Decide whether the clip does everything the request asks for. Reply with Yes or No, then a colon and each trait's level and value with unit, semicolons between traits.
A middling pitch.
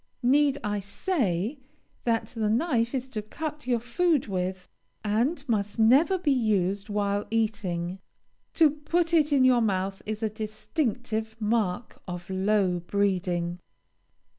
No: high, 220 Hz